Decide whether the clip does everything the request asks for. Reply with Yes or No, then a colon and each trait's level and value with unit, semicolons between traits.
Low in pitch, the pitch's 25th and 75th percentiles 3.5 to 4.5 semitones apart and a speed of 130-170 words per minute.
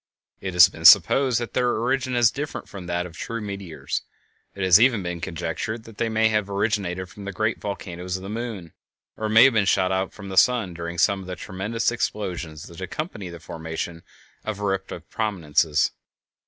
No: low, 100 Hz; average, 4.0 semitones; average, 195 wpm